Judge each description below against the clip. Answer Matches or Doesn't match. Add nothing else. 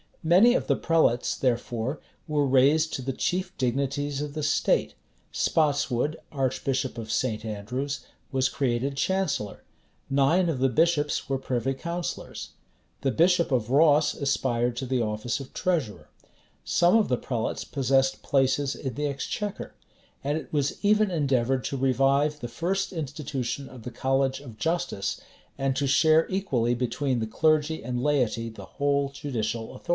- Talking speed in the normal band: Matches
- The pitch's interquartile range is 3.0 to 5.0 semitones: Matches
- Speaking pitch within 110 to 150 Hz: Matches